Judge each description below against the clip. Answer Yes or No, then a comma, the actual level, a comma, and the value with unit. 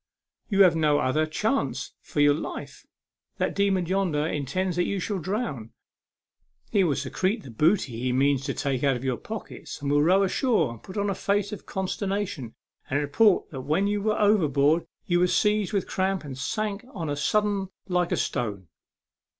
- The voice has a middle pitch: Yes, medium, 175 Hz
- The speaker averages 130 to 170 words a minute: No, average, 185 wpm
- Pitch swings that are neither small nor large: No, wide, 5.9 semitones